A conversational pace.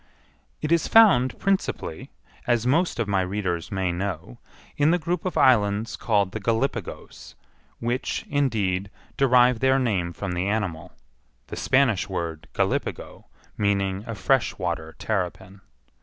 No: slow, 130 wpm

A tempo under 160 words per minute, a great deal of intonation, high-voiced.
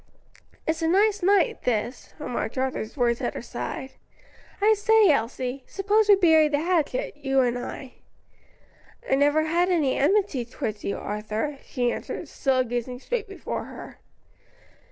Yes: average, 150 wpm; wide, 7.7 semitones; very high, 290 Hz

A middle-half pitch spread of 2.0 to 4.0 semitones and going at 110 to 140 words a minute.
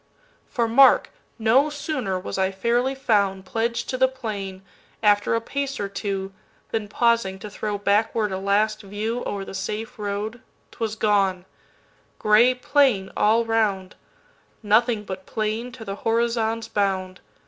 Yes: average, 2.8 semitones; slow, 135 wpm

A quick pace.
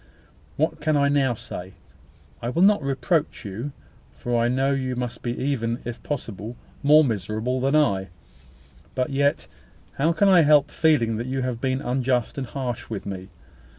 No: average, 170 wpm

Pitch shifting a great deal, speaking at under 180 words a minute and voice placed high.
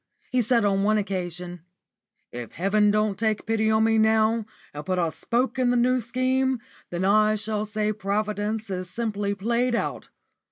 No: narrow, 2.5 semitones; average, 170 wpm; high, 215 Hz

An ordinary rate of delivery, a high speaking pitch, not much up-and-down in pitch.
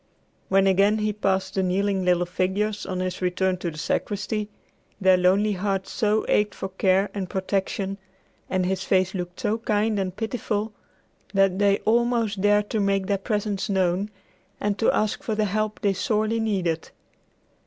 Yes: average, 165 wpm; high, 195 Hz; narrow, 1.9 semitones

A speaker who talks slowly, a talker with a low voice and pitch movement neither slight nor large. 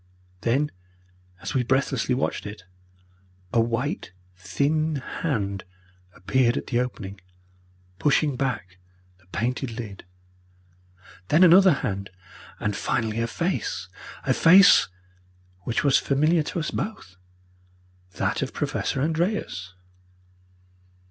No: slow, 110 wpm; low, 125 Hz; wide, 6.7 semitones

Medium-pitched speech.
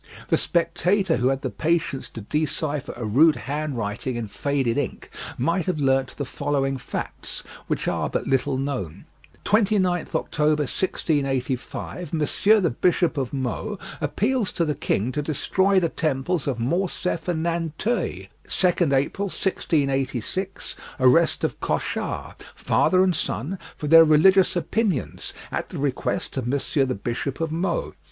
Yes: medium, 150 Hz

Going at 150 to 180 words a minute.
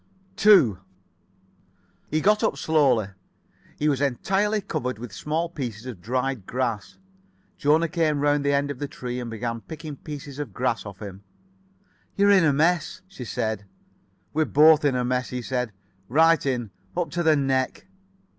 Yes: average, 165 wpm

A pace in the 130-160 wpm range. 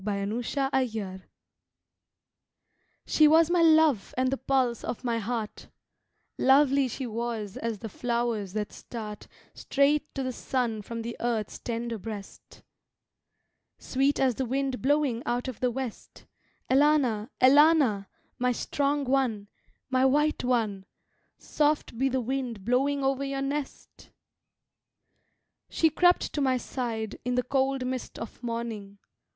Yes: slow, 135 wpm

